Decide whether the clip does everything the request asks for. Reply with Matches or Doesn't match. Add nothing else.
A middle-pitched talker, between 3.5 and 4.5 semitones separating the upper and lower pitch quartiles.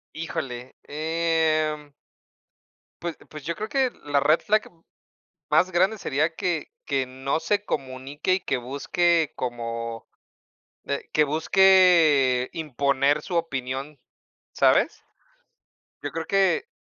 Matches